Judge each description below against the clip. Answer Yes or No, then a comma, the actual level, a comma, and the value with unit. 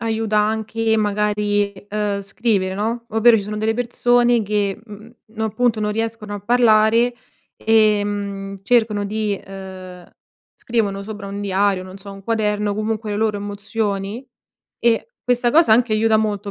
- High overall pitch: Yes, high, 215 Hz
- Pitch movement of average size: No, narrow, 1.8 semitones